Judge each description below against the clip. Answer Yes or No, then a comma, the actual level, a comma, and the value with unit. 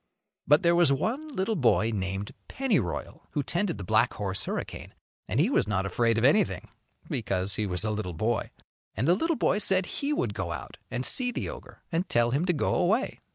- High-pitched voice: No, low, 135 Hz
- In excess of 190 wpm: Yes, fast, 205 wpm